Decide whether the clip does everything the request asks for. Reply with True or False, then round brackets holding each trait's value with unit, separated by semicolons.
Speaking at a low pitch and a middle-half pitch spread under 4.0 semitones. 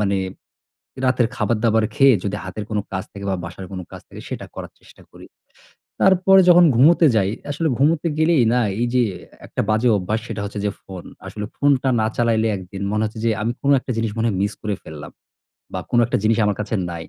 False (110 Hz; 4.3 semitones)